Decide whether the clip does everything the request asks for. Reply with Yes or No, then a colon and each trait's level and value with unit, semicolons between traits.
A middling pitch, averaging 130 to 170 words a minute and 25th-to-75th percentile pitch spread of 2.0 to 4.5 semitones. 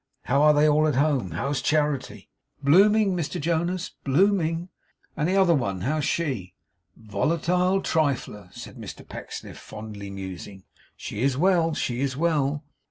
No: medium, 150 Hz; average, 145 wpm; wide, 5.4 semitones